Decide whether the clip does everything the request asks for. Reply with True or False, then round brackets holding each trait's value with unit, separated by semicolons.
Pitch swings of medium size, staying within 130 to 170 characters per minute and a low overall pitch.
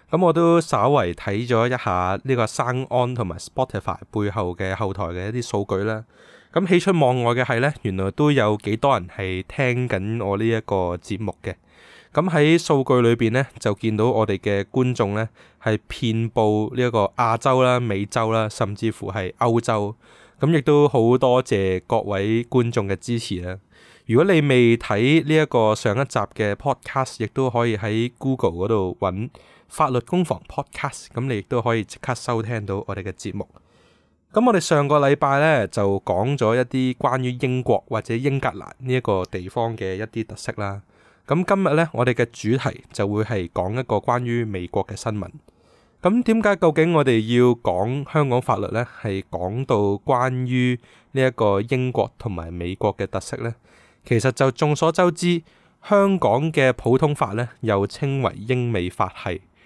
False (4.2 semitones; 275 characters per minute; 120 Hz)